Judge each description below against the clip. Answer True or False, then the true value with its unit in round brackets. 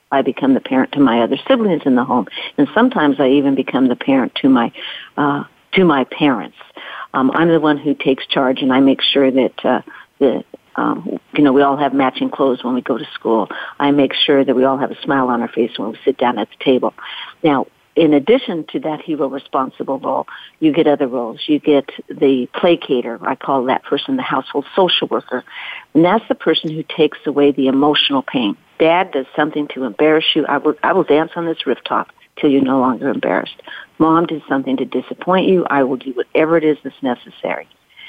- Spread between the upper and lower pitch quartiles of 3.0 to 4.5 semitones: True (3.4 semitones)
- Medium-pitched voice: True (145 Hz)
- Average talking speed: False (215 wpm)